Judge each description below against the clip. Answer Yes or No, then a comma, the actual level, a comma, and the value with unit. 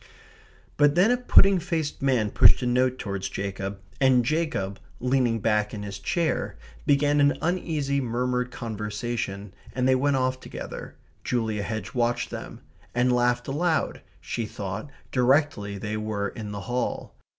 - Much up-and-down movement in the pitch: No, average, 4.9 semitones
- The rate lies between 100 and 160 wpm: Yes, average, 150 wpm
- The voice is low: Yes, low, 125 Hz